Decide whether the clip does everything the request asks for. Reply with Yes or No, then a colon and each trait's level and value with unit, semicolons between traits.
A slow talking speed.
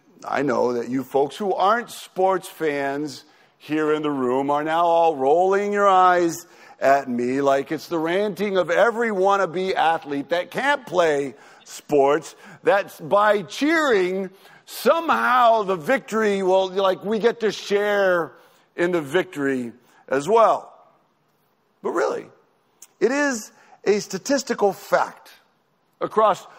Yes: slow, 130 wpm